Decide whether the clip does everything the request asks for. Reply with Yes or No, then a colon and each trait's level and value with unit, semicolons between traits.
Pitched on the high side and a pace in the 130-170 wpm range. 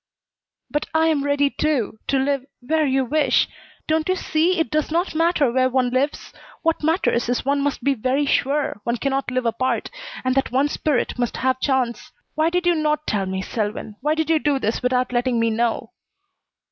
No: very high, 275 Hz; average, 195 wpm